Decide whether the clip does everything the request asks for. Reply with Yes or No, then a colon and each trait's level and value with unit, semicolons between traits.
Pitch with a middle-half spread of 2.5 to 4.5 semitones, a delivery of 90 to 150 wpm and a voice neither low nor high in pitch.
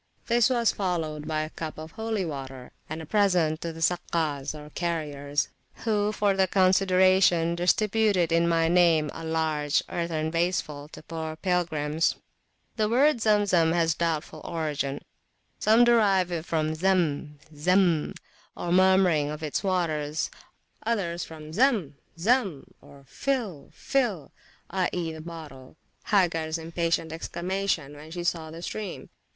Yes: average, 3.5 semitones; average, 140 wpm; medium, 170 Hz